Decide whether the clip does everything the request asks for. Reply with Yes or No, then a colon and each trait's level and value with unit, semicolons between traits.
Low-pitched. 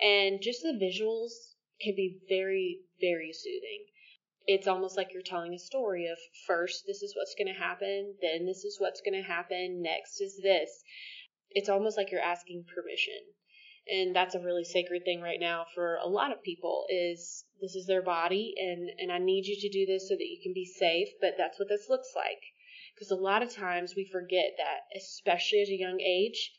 No: high, 195 Hz